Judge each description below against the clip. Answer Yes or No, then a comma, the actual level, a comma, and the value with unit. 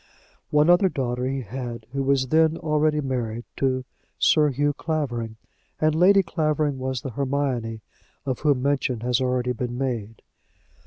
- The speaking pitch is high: No, low, 135 Hz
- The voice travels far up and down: No, average, 3.4 semitones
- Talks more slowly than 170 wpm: Yes, average, 150 wpm